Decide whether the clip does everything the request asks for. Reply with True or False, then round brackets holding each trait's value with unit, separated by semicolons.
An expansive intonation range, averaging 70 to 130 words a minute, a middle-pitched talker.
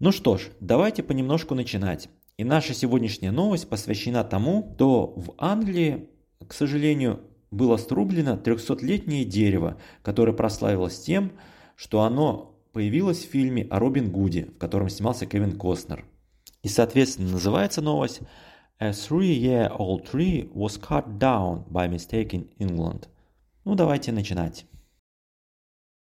False (7.2 semitones; 125 wpm; 115 Hz)